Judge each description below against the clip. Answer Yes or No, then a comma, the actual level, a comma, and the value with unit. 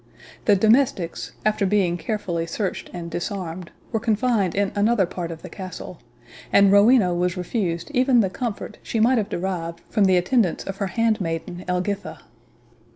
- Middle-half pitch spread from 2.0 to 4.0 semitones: Yes, average, 3.6 semitones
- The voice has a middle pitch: No, high, 195 Hz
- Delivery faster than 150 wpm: Yes, average, 160 wpm